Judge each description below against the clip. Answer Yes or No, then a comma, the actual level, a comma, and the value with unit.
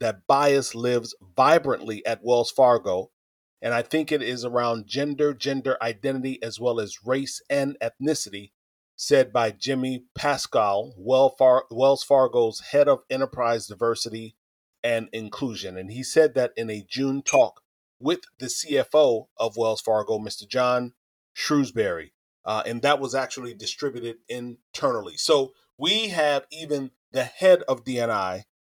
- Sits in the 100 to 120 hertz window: No, low, 130 Hz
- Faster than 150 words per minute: No, average, 140 wpm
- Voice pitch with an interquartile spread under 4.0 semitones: Yes, average, 3.2 semitones